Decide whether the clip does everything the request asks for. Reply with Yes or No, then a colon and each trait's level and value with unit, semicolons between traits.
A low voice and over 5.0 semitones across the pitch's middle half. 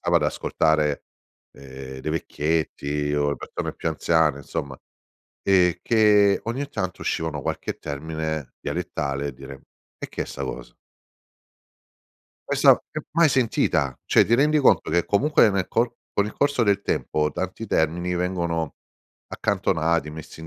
Yes: very low, 80 Hz; wide, 5.4 semitones